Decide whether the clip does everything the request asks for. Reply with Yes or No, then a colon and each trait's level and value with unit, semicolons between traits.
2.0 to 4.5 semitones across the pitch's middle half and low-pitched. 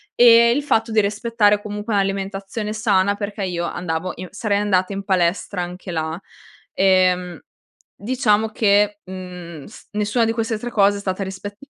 No: narrow, 2.5 semitones; high, 200 Hz